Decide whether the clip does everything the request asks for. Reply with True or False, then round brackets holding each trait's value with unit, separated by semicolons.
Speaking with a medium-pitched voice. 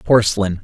False (105 Hz)